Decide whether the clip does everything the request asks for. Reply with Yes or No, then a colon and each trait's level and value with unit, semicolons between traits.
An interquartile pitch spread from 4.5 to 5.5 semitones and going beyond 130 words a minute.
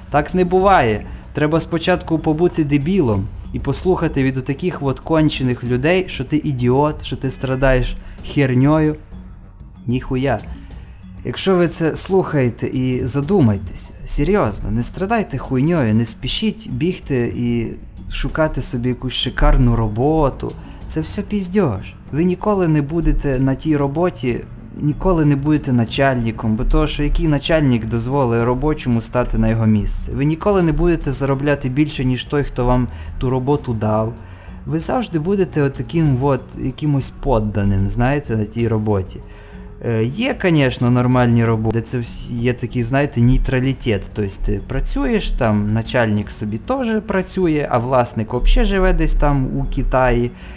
Yes: average, 4.9 semitones; average, 140 wpm